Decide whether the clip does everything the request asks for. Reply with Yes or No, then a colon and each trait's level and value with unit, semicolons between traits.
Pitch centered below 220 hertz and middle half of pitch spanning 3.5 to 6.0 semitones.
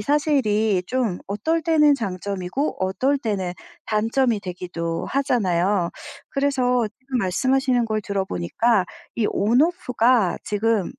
No: high, 225 Hz; wide, 5.6 semitones